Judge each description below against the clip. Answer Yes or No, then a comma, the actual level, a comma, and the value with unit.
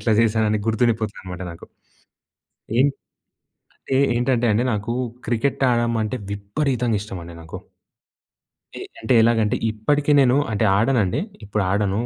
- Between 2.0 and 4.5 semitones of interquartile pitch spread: Yes, average, 2.9 semitones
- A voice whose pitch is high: No, low, 110 Hz